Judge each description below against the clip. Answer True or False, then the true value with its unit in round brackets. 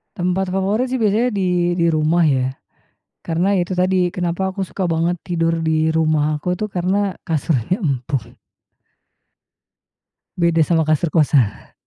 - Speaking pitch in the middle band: True (175 Hz)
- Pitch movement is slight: False (3.0 semitones)